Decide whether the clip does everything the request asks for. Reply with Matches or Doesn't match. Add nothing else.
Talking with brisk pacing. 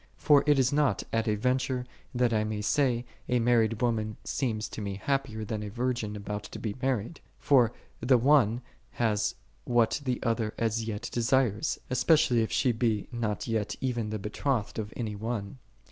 Doesn't match